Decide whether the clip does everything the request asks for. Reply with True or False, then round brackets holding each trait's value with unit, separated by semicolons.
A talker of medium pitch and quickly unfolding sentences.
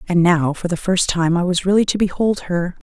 True (180 Hz; 245 wpm)